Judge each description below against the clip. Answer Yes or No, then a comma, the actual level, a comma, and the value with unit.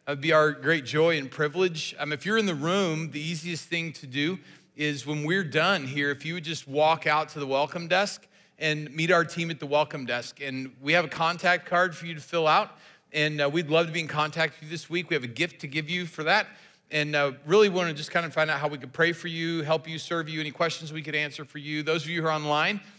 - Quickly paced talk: Yes, fast, 280 wpm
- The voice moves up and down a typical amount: No, narrow, 2.2 semitones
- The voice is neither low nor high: Yes, medium, 160 Hz